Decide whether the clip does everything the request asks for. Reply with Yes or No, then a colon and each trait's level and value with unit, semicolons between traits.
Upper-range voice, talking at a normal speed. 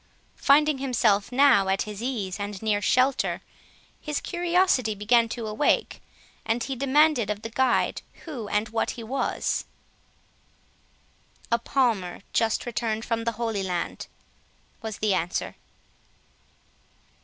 No: high, 230 Hz; slow, 125 wpm